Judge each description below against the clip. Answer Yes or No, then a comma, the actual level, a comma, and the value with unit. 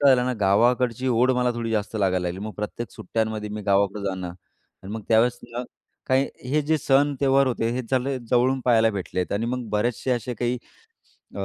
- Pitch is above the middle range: No, low, 115 Hz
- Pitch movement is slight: No, average, 3.4 semitones